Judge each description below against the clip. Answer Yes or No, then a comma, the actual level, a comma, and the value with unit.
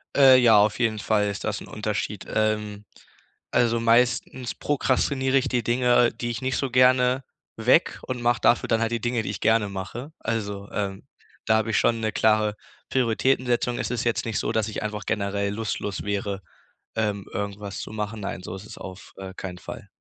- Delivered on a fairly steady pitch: No, average, 3.0 semitones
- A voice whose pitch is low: Yes, low, 110 Hz